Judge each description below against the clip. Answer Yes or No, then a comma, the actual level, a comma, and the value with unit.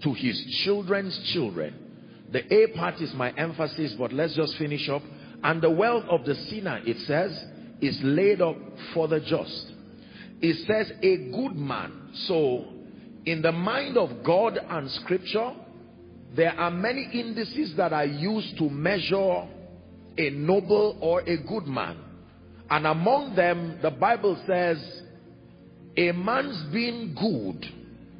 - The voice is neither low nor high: Yes, medium, 170 Hz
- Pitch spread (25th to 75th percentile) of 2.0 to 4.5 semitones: No, wide, 5.5 semitones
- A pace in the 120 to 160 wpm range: Yes, average, 145 wpm